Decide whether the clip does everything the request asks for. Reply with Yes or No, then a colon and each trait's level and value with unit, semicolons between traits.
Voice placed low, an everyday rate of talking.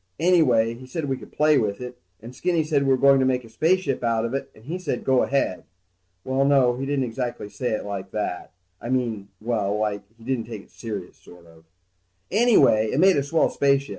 No: low, 125 Hz; fast, 225 wpm